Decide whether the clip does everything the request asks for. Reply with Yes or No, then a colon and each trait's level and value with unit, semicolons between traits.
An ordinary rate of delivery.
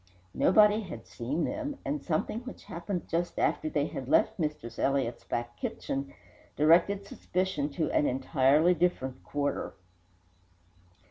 No: slow, 130 wpm